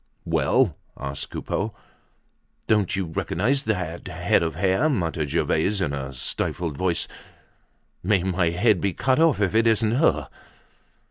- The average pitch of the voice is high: No, very low, 95 Hz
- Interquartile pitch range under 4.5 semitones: No, average, 5.0 semitones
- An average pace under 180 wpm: Yes, average, 140 wpm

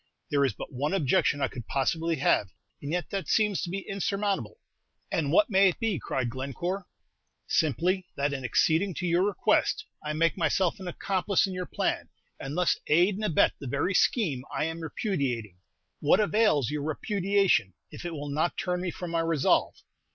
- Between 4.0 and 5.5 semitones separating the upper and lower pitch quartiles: Yes, average, 5.2 semitones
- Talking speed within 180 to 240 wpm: Yes, average, 185 wpm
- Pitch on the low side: No, medium, 165 Hz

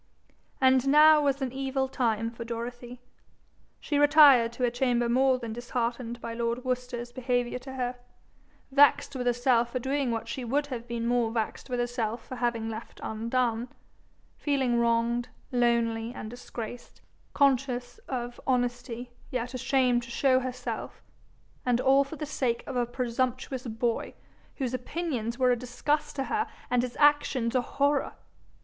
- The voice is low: No, high, 245 Hz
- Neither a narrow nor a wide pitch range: No, narrow, 2.0 semitones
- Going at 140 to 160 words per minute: Yes, average, 155 wpm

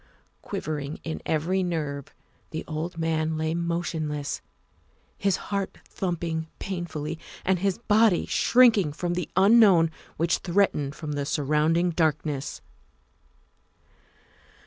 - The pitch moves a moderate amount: Yes, average, 3.0 semitones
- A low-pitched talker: No, medium, 165 Hz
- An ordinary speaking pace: No, slow, 110 wpm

